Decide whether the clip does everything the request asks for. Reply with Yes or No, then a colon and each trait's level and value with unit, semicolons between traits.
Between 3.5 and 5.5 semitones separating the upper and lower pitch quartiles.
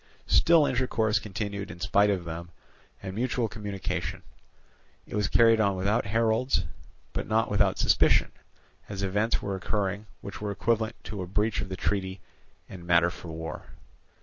No: average, 2.7 semitones